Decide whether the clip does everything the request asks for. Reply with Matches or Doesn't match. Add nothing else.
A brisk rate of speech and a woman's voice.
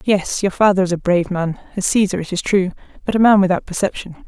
Matches